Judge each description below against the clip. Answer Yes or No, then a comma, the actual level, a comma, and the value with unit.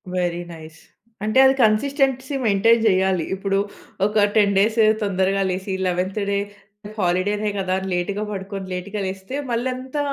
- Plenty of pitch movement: No, narrow, 2.6 semitones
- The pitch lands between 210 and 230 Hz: No, high, 200 Hz